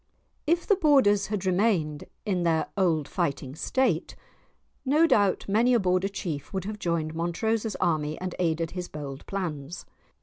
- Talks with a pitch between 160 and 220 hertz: Yes, medium, 185 Hz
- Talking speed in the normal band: Yes, average, 155 wpm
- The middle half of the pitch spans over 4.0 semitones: Yes, average, 4.7 semitones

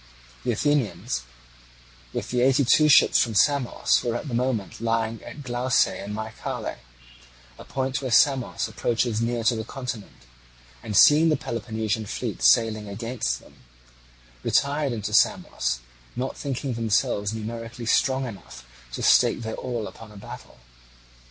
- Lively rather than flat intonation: No, average, 3.1 semitones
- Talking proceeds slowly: No, average, 145 wpm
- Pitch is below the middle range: Yes, low, 115 Hz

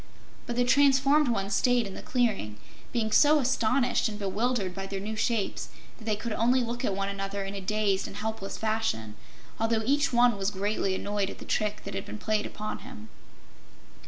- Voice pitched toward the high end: Yes, high, 215 Hz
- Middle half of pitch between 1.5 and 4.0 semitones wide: Yes, average, 3.5 semitones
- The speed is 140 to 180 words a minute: No, average, 195 wpm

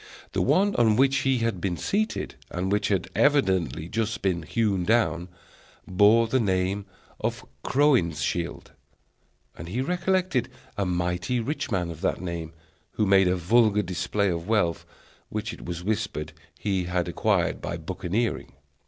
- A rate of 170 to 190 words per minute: No, average, 150 wpm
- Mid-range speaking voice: No, low, 100 Hz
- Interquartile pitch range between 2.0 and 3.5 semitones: No, average, 4.7 semitones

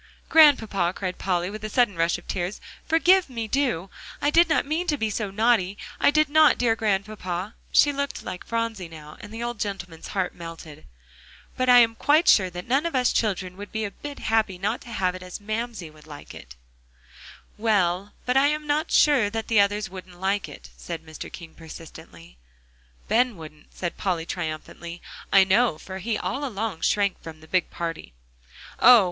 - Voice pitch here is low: No, high, 205 Hz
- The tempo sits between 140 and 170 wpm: No, average, 190 wpm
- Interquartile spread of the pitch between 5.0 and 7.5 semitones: Yes, average, 5.3 semitones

